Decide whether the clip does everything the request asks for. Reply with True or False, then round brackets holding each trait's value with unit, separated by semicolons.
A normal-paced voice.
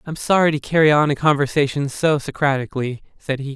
True (185 wpm)